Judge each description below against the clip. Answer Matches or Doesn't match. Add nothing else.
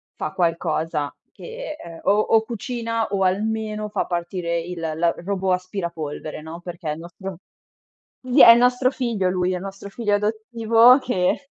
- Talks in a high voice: Matches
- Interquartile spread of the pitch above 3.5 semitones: Matches